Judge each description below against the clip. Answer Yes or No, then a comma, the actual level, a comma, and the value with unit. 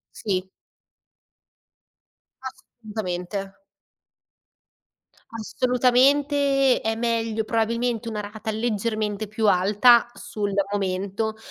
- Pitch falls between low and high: No, high, 220 Hz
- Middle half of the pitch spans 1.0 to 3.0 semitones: Yes, average, 2.7 semitones